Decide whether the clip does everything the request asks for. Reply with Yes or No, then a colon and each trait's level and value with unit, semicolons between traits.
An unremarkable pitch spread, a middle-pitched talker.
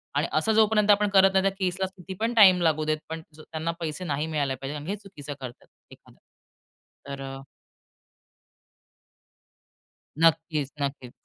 Yes: average, 4.7 semitones; medium, 165 Hz